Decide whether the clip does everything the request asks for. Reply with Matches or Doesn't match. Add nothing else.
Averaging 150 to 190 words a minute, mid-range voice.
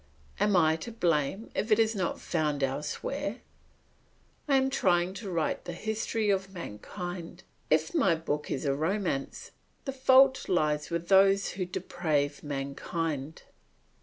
Doesn't match